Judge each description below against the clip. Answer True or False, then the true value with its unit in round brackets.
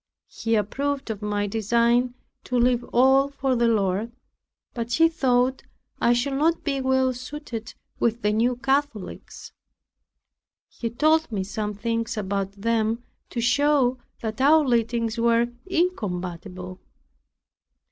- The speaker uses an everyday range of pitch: True (3.6 semitones)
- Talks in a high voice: True (235 Hz)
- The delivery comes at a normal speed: False (125 wpm)